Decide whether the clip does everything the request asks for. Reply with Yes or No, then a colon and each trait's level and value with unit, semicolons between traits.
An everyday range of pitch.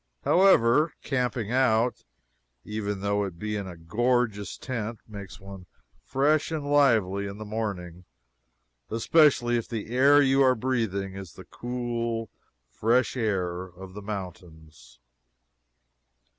Yes: average, 4.3 semitones